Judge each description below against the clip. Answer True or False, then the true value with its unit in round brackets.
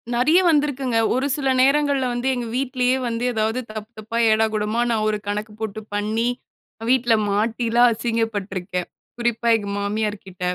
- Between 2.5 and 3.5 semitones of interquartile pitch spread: True (2.8 semitones)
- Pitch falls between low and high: False (225 Hz)